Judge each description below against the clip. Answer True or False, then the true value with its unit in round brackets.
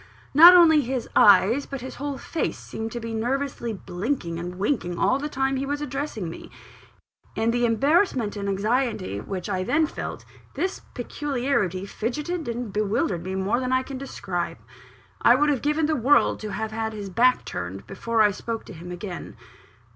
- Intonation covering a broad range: True (5.7 semitones)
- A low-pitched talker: False (235 Hz)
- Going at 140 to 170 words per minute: False (180 wpm)